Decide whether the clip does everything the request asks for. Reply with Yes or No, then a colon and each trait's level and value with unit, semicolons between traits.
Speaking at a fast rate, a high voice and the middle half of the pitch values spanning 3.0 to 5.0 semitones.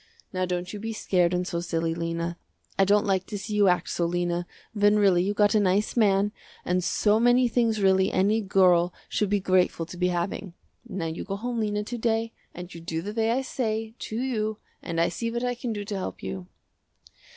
Yes: fast, 220 wpm; high, 195 Hz; average, 3.5 semitones